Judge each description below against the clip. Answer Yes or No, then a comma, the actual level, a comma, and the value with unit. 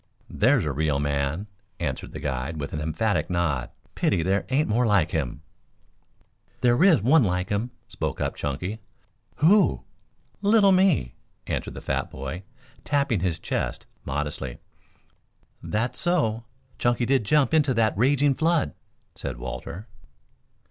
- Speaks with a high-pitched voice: No, low, 100 Hz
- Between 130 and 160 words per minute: Yes, slow, 135 wpm